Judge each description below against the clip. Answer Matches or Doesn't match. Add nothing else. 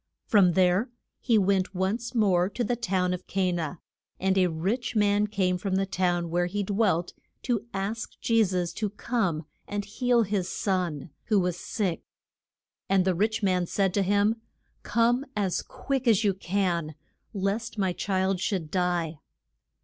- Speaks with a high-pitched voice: Matches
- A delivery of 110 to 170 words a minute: Matches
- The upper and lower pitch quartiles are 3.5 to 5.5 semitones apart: Doesn't match